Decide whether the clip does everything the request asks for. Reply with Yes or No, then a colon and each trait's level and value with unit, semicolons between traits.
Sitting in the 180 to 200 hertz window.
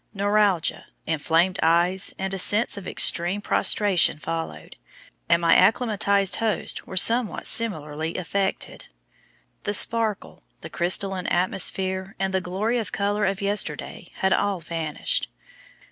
Yes: high, 190 Hz